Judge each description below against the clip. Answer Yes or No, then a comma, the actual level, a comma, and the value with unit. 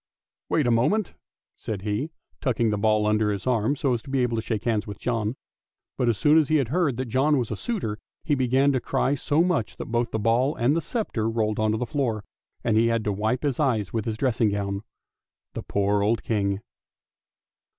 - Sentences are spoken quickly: Yes, fast, 225 wpm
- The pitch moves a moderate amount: Yes, average, 3.9 semitones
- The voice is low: Yes, low, 115 Hz